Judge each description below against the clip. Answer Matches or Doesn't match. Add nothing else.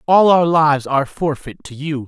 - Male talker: Matches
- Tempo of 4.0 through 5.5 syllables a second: Matches